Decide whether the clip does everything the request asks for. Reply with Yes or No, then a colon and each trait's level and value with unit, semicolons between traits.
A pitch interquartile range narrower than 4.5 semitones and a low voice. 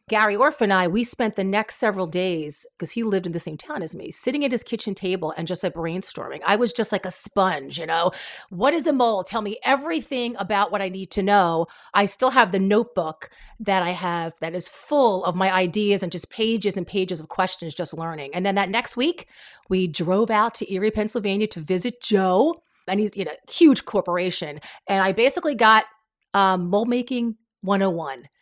No: average, 3.8 semitones; high, 200 Hz